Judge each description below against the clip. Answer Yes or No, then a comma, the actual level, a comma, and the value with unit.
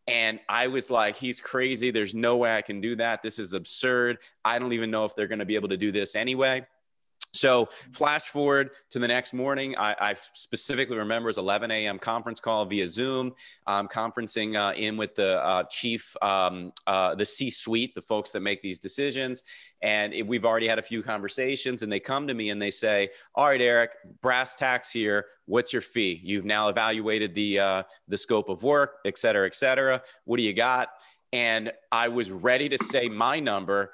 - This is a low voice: Yes, low, 115 Hz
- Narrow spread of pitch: No, average, 3.5 semitones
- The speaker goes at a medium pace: No, fast, 210 wpm